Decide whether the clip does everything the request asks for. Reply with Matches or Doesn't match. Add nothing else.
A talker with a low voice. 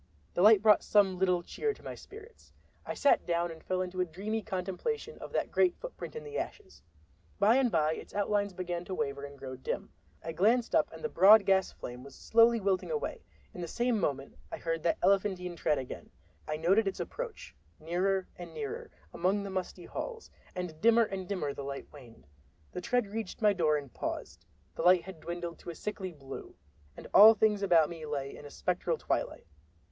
Doesn't match